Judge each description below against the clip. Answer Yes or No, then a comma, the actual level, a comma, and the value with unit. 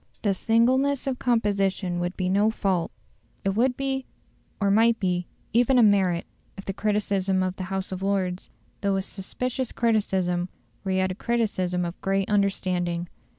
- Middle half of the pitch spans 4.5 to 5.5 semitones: No, average, 3.4 semitones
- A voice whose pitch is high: Yes, high, 195 Hz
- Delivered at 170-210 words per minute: No, average, 160 wpm